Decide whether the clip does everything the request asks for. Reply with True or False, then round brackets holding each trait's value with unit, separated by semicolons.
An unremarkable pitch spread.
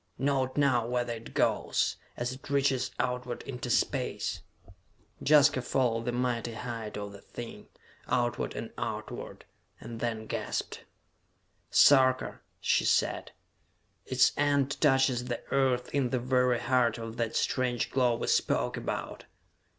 False (1.9 semitones)